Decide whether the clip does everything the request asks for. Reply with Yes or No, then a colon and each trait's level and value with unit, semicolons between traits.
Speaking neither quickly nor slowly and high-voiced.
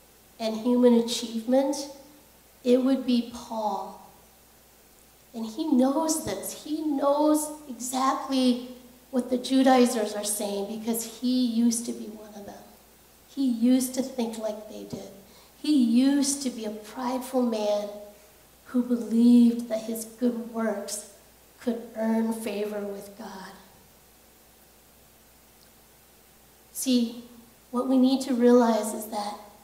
No: slow, 120 wpm; high, 240 Hz